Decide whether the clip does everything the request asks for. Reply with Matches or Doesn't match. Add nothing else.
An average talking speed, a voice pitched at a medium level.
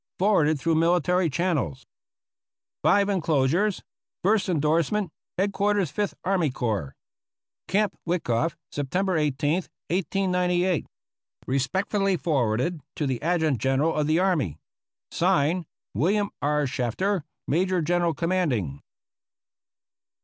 Doesn't match